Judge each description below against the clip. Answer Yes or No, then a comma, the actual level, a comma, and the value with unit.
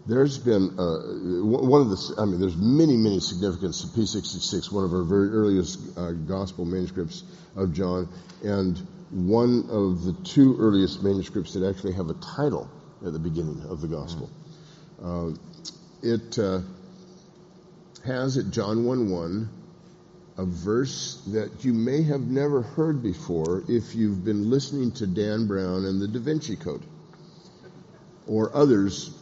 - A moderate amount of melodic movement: No, wide, 8.2 semitones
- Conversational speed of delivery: Yes, average, 150 wpm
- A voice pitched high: No, low, 110 Hz